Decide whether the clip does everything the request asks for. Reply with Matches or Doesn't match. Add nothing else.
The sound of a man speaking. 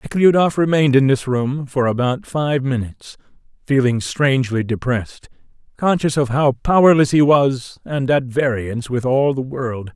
Matches